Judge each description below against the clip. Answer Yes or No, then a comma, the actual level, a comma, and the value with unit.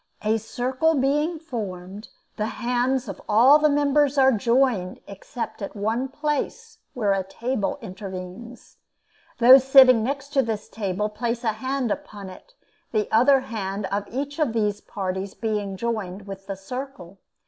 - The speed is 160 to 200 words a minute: No, average, 150 wpm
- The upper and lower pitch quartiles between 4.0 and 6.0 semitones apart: Yes, average, 4.9 semitones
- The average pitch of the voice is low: No, high, 230 Hz